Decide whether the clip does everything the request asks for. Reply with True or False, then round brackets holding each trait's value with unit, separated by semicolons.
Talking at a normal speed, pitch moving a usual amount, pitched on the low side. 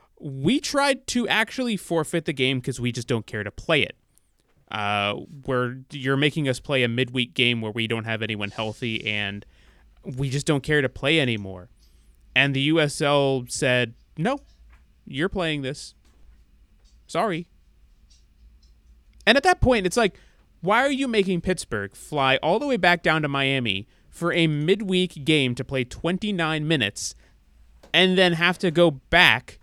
False (160 wpm; 8.5 semitones; 130 Hz)